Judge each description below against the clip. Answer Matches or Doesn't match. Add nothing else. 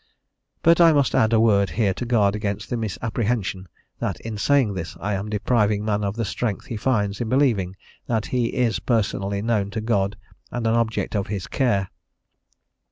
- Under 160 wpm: Doesn't match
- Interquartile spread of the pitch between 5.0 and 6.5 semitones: Doesn't match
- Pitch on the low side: Matches